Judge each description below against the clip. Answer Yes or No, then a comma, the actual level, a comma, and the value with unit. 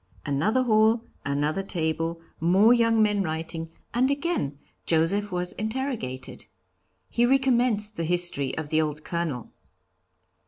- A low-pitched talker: No, medium, 180 Hz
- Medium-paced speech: No, slow, 120 wpm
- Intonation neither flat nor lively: No, wide, 6.2 semitones